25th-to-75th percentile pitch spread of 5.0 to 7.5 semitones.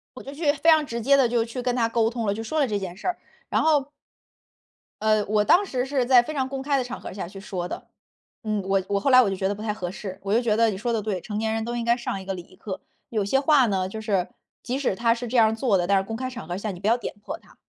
No: average, 4.2 semitones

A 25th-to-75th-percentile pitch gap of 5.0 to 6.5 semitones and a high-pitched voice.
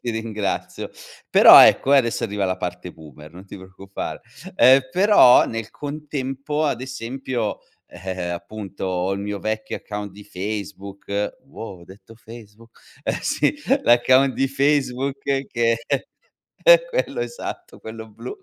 No: average, 5.3 semitones; low, 110 Hz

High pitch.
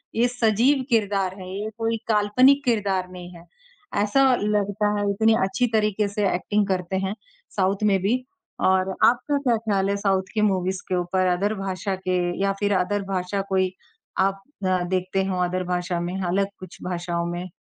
Yes: high, 195 Hz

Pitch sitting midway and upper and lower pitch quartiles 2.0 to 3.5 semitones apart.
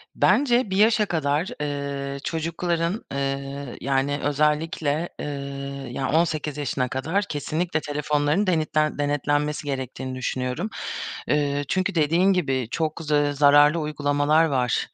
Yes: medium, 150 Hz; narrow, 2.6 semitones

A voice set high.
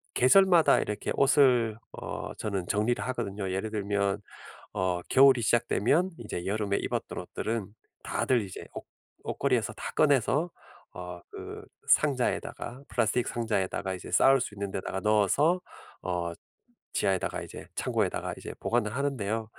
No: low, 110 Hz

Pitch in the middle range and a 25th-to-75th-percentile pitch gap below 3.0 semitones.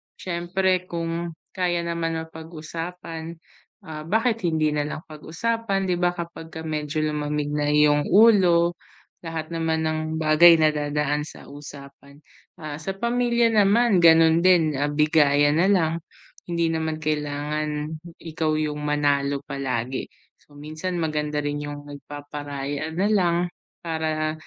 Yes: medium, 160 Hz; narrow, 2.5 semitones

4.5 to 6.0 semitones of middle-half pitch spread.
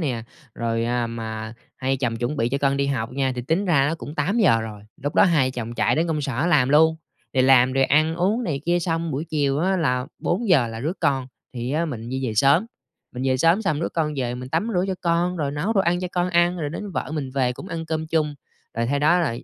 Yes: average, 4.8 semitones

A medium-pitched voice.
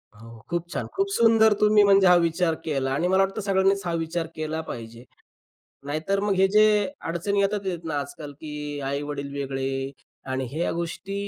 Yes: medium, 165 Hz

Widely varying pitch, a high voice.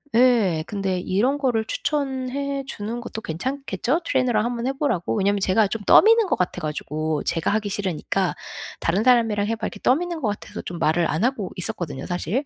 Yes: wide, 5.9 semitones; high, 220 Hz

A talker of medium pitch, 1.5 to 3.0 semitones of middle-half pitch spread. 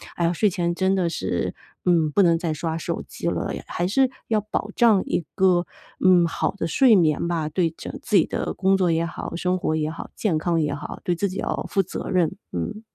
Yes: medium, 175 Hz; average, 2.7 semitones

